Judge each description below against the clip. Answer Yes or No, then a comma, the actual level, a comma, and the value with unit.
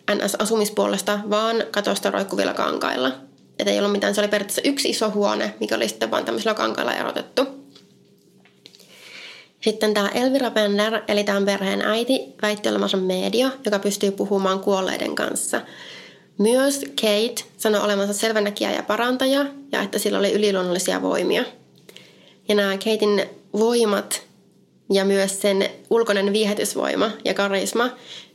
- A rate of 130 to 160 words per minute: Yes, average, 135 wpm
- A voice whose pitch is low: No, high, 210 Hz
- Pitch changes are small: Yes, narrow, 2.0 semitones